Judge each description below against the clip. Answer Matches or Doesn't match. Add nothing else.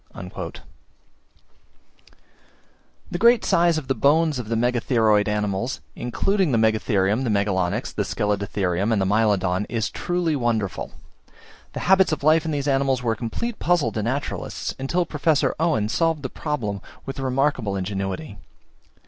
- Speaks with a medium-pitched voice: Doesn't match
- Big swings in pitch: Matches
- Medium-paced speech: Doesn't match